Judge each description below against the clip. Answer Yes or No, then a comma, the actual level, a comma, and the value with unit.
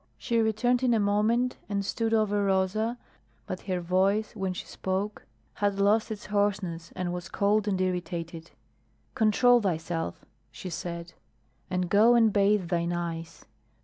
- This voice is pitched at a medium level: No, high, 200 Hz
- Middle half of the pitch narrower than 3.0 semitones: No, average, 3.3 semitones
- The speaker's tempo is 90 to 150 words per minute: Yes, average, 145 wpm